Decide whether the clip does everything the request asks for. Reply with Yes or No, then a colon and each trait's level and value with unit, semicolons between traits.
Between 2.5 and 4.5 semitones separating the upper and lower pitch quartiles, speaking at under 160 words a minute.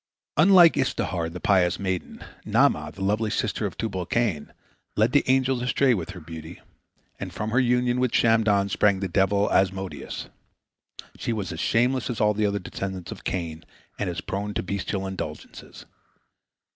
No: average, 4.0 semitones; average, 165 wpm